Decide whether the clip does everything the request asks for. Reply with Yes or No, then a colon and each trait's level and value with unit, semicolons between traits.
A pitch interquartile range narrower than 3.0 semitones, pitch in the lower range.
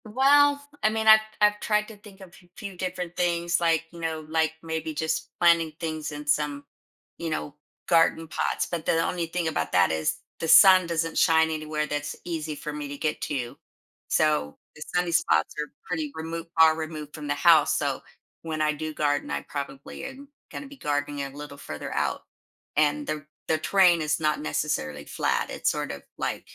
No: narrow, 2.6 semitones; medium, 160 Hz